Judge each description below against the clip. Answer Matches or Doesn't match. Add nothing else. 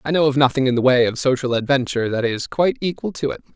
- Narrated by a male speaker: Matches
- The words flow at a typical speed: Doesn't match